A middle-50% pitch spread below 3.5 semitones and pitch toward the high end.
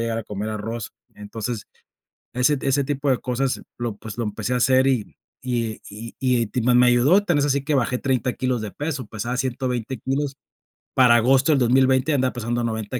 No: narrow, 2.5 semitones; low, 125 Hz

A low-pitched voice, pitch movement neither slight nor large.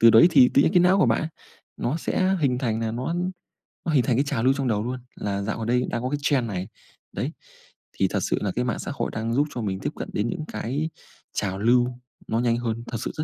Yes: low, 125 Hz; average, 4.0 semitones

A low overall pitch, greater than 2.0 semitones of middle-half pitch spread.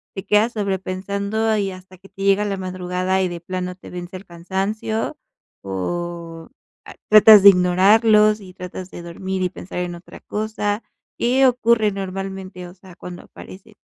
No: high, 190 Hz; narrow, 2.4 semitones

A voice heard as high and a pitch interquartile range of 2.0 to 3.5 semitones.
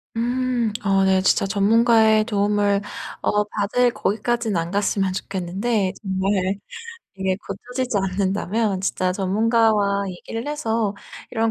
Yes: high, 205 Hz; average, 2.9 semitones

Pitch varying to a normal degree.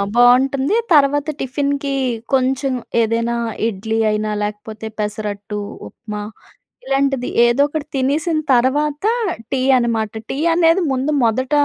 Yes: average, 4.2 semitones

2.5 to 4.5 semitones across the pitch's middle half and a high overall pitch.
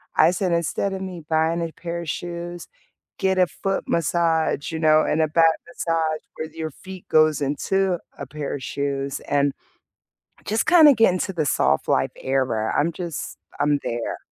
No: average, 2.9 semitones; medium, 165 Hz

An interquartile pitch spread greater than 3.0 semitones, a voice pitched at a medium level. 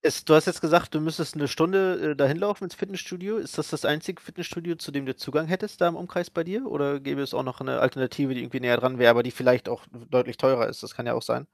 Yes: average, 5.0 semitones; medium, 155 Hz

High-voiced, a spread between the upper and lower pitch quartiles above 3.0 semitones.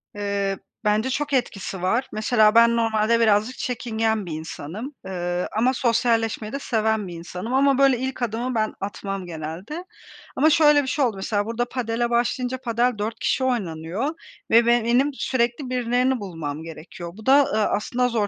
Yes: high, 230 Hz; average, 3.7 semitones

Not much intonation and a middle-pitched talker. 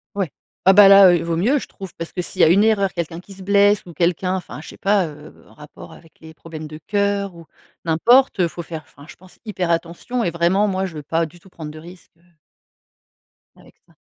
No: average, 3.2 semitones; medium, 180 Hz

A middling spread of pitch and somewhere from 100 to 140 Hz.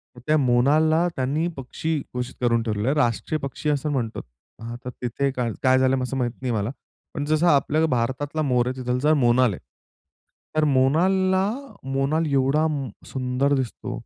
Yes: average, 3.5 semitones; low, 135 Hz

